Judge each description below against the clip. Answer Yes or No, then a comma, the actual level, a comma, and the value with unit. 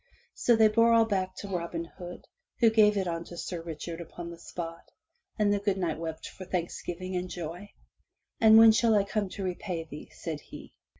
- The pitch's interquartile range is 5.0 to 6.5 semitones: No, average, 3.7 semitones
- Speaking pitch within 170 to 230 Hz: Yes, medium, 185 Hz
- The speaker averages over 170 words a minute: Yes, average, 200 wpm